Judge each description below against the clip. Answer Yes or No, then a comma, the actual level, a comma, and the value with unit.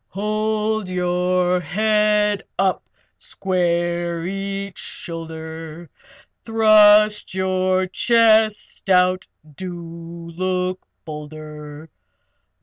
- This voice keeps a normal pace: No, slow, 65 wpm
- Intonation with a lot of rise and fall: No, average, 3.5 semitones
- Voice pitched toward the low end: No, medium, 185 Hz